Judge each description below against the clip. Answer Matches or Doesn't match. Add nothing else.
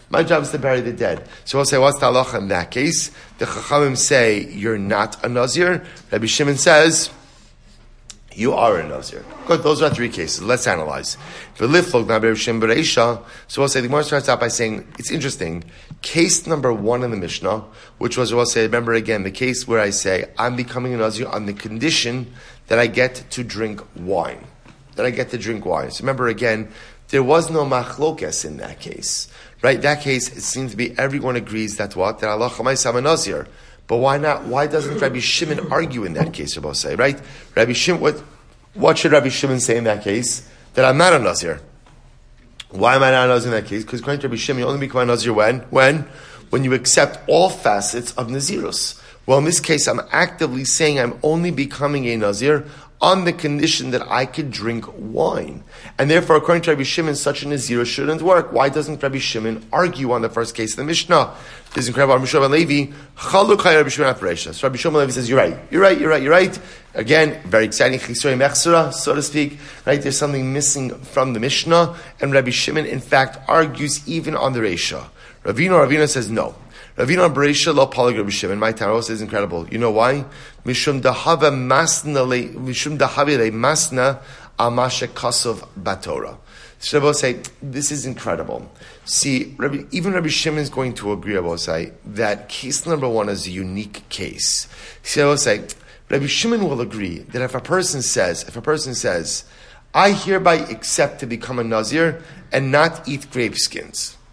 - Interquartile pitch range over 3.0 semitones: Matches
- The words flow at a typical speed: Matches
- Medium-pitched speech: Doesn't match